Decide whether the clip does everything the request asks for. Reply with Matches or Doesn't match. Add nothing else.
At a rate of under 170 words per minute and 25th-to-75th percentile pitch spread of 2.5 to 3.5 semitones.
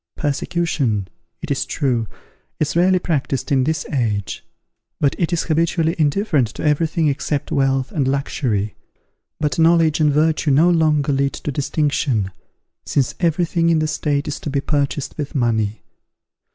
Matches